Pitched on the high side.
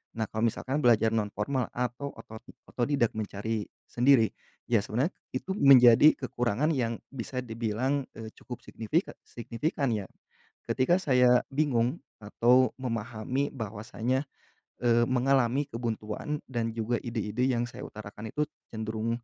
No: low, 120 Hz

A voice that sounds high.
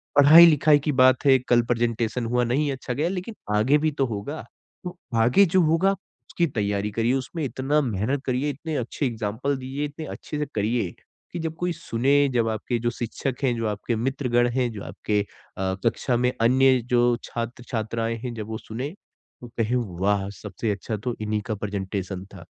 No: low, 125 Hz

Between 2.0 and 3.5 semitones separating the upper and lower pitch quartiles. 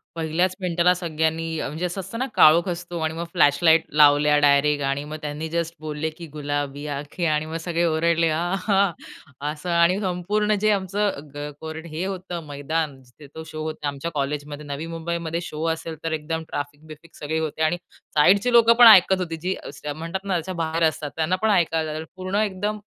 Yes: average, 3.0 semitones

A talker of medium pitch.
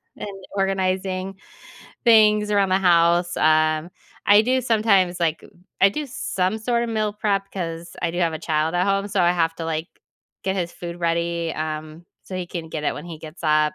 Yes: medium, 180 Hz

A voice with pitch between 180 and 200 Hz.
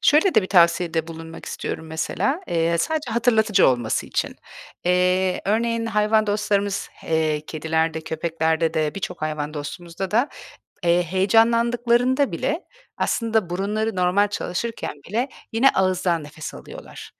Yes: medium, 185 Hz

